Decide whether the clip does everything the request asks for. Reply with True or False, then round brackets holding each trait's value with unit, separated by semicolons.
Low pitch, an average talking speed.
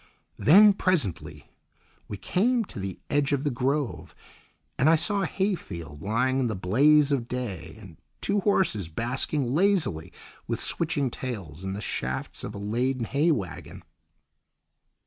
True (130 Hz; 145 wpm)